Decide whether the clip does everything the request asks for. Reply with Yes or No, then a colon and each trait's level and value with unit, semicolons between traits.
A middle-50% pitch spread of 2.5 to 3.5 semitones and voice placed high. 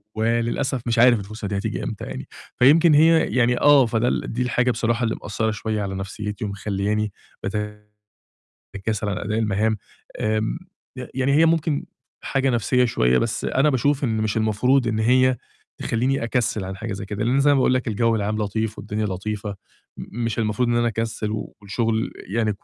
No: average, 3.1 semitones; low, 110 Hz